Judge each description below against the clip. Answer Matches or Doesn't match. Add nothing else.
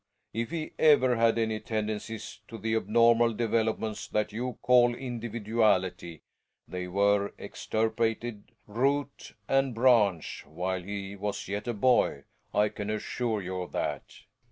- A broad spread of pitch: Doesn't match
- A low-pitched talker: Matches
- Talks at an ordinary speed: Doesn't match